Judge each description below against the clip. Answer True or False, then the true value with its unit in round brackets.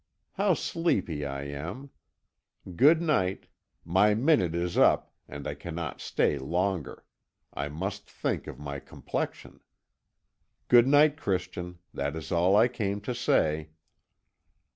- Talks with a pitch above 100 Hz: False (90 Hz)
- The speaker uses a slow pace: True (120 wpm)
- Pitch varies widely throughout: True (7.6 semitones)